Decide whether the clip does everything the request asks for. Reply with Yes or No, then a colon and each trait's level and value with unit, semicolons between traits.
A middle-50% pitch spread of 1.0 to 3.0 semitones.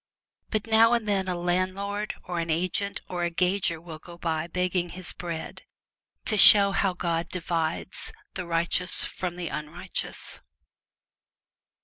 Yes: narrow, 2.4 semitones